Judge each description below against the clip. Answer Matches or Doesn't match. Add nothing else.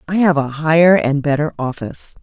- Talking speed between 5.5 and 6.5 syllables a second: Matches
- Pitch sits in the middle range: Matches